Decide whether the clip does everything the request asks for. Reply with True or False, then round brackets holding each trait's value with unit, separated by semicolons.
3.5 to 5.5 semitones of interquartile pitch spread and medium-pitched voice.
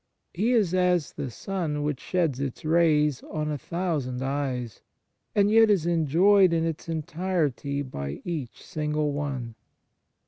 True (4.0 semitones; 155 Hz)